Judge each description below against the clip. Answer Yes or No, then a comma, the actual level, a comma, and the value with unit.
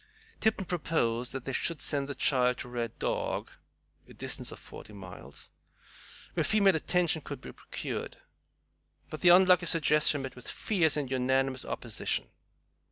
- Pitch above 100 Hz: Yes, medium, 140 Hz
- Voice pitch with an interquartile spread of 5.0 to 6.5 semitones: Yes, average, 5.3 semitones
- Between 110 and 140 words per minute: No, average, 150 wpm